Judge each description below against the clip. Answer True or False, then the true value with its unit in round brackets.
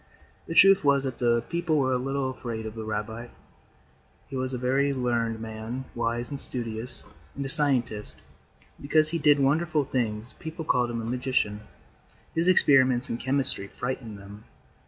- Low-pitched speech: True (125 Hz)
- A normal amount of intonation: True (3.4 semitones)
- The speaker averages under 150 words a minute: False (170 wpm)